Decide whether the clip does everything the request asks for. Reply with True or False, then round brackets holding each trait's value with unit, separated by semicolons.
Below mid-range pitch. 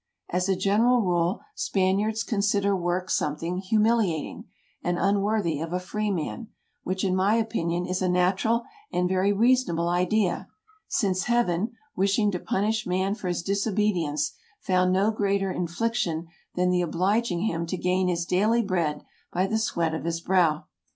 False (185 Hz)